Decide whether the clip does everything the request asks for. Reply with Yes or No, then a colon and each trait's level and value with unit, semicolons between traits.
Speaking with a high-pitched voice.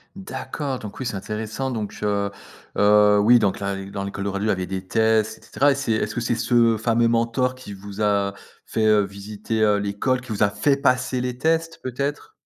No: low, 110 Hz